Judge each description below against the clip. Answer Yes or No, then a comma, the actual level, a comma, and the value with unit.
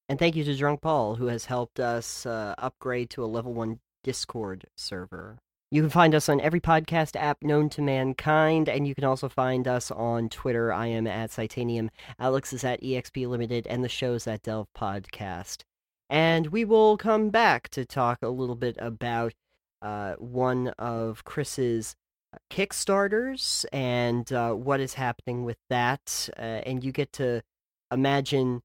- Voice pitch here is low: Yes, low, 125 Hz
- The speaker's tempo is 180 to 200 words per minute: No, average, 170 wpm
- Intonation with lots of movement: No, average, 3.6 semitones